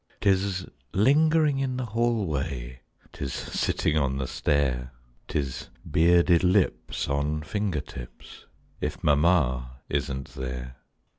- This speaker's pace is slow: Yes, slow, 105 wpm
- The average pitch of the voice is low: Yes, very low, 75 Hz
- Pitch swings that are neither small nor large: No, wide, 6.9 semitones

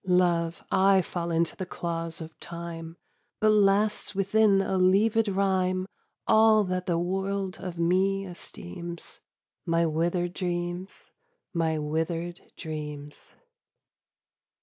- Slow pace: Yes, slow, 110 wpm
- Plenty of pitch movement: No, narrow, 2.5 semitones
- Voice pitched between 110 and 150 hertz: No, medium, 180 Hz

